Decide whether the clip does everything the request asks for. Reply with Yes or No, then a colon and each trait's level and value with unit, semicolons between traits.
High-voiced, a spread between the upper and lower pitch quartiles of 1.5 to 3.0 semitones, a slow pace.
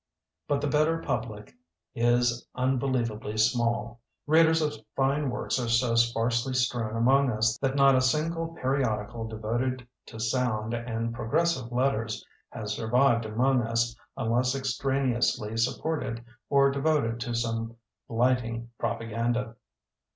No: low, 120 Hz; average, 2.7 semitones; slow, 130 wpm